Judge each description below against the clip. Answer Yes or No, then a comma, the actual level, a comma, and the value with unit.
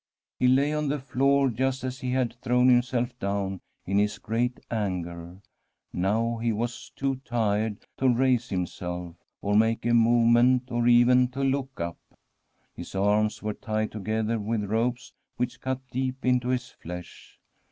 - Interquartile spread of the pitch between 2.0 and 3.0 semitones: No, average, 3.4 semitones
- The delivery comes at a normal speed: Yes, average, 155 wpm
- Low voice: Yes, low, 120 Hz